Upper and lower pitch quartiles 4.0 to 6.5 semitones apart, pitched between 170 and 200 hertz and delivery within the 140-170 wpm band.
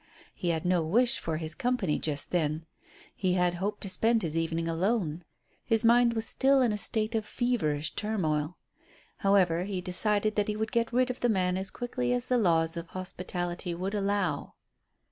No: average, 4.9 semitones; medium, 185 Hz; average, 185 wpm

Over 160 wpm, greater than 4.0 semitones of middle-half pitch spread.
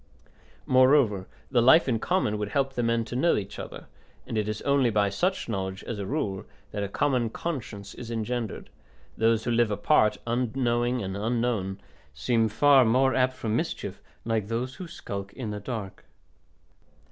No: average, 170 wpm; average, 3.6 semitones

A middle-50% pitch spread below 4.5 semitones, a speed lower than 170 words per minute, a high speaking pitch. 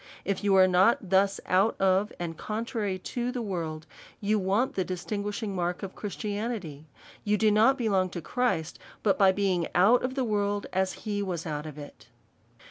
No: average, 2.7 semitones; average, 180 wpm; high, 195 Hz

